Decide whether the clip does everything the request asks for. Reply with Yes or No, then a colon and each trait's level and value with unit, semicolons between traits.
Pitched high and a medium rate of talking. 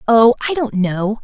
Yes: high, 225 Hz; average, 195 wpm